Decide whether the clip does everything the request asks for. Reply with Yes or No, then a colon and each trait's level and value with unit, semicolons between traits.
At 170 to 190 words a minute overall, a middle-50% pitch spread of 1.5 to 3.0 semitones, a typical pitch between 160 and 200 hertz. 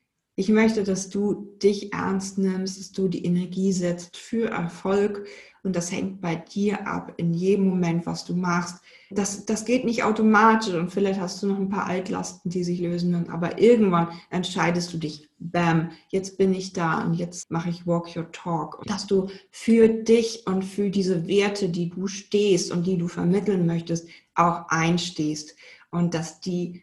Yes: average, 185 wpm; average, 2.7 semitones; medium, 185 Hz